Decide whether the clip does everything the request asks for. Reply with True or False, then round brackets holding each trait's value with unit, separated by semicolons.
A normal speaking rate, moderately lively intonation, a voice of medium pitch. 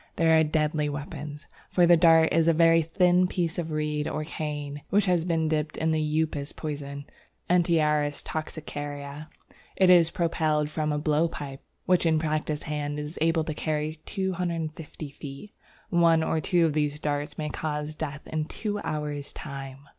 False (170 wpm; 1.8 semitones; 155 Hz)